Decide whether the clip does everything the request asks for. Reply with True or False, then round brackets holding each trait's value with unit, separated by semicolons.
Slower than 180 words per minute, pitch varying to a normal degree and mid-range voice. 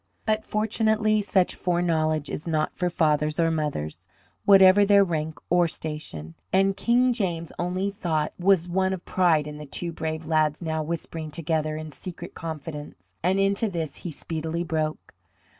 True (160 wpm; 3.5 semitones; 165 Hz)